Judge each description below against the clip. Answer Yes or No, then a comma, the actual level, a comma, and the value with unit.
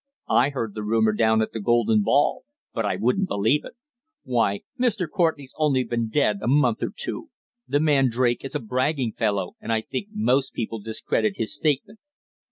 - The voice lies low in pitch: Yes, low, 120 Hz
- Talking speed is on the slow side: No, average, 185 wpm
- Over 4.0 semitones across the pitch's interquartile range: Yes, average, 4.8 semitones